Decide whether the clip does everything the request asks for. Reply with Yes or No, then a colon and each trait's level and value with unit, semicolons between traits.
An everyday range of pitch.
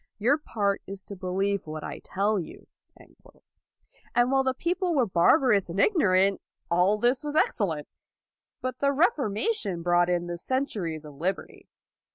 No: wide, 6.8 semitones